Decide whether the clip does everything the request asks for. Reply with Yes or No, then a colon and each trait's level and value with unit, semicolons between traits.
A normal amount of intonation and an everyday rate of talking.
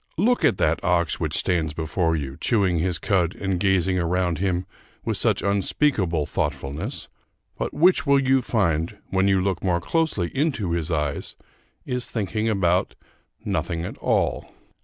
Yes: average, 3.9 semitones; average, 155 wpm